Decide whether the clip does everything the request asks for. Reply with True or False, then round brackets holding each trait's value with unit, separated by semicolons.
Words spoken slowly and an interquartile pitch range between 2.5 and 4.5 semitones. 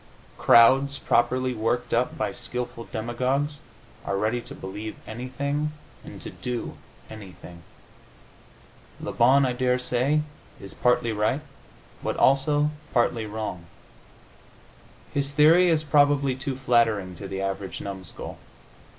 True (115 wpm; 4.1 semitones)